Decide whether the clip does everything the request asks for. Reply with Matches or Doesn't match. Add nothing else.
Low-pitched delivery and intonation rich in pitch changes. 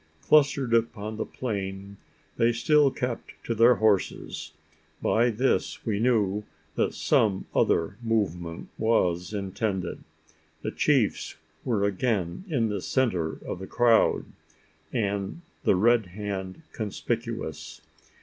Doesn't match